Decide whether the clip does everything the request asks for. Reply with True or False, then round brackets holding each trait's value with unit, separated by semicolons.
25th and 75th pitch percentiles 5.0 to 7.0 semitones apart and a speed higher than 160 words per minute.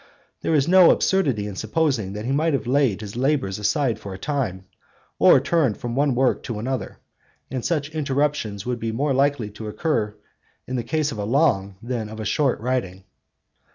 True (5.3 semitones; 190 wpm)